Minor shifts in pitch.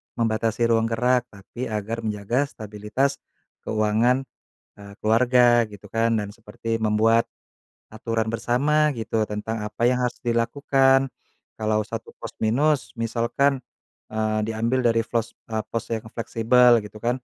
Yes: narrow, 2.2 semitones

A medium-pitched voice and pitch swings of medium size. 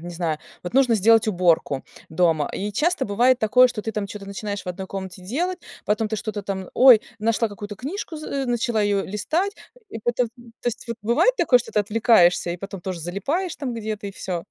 No: high, 215 Hz; average, 4.2 semitones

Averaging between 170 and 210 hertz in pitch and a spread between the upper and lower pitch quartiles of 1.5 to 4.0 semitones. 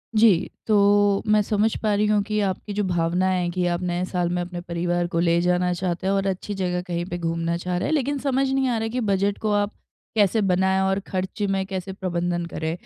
Yes: medium, 185 Hz; average, 2.7 semitones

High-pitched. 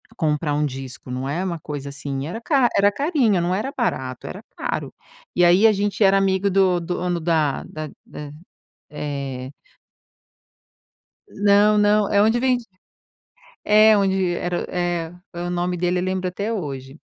No: medium, 180 Hz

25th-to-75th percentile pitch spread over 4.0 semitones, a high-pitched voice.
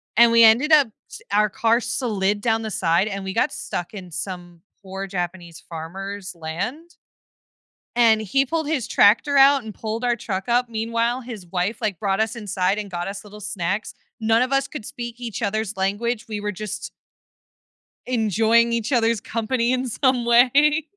No: average, 3.6 semitones; high, 220 Hz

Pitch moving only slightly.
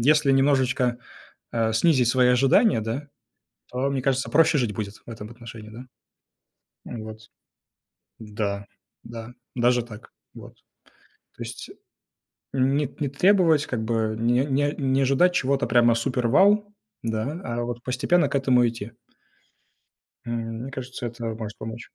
No: average, 3.1 semitones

